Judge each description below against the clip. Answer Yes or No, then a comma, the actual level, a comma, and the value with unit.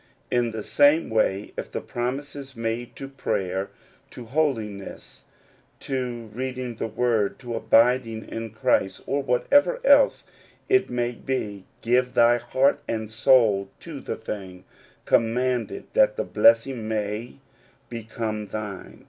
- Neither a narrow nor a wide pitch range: Yes, average, 3.2 semitones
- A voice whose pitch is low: Yes, low, 120 Hz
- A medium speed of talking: No, slow, 130 wpm